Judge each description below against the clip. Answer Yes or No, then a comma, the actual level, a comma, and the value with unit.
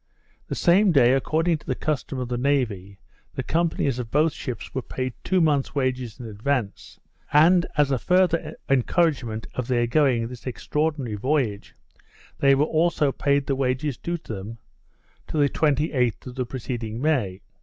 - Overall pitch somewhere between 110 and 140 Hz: Yes, low, 135 Hz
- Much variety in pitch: No, average, 4.2 semitones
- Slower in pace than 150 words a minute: No, average, 165 wpm